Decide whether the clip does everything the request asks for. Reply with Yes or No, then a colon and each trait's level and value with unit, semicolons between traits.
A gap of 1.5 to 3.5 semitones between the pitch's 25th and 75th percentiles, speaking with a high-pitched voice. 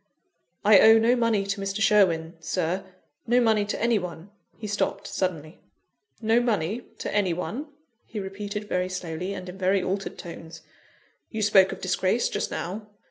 Yes: average, 3.0 semitones; high, 195 Hz